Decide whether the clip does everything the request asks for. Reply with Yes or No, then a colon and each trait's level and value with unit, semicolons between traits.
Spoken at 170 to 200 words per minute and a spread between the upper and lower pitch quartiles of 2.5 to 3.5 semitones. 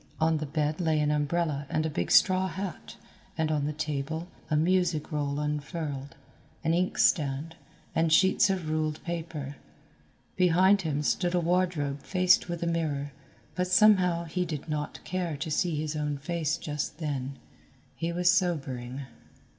No: average, 160 wpm; average, 3.0 semitones